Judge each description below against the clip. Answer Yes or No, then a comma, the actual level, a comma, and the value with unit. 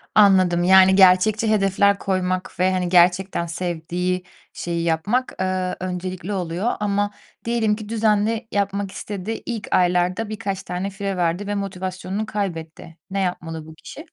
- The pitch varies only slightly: Yes, narrow, 2.3 semitones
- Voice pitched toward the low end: No, high, 190 Hz